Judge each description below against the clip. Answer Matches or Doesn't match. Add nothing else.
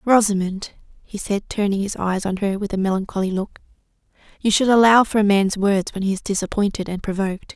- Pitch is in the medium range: Doesn't match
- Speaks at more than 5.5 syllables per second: Matches